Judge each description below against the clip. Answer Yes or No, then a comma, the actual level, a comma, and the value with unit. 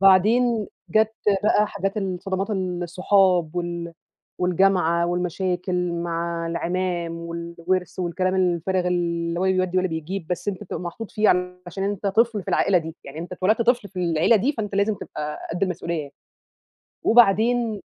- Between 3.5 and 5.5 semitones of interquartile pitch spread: No, narrow, 2.5 semitones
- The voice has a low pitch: No, medium, 180 Hz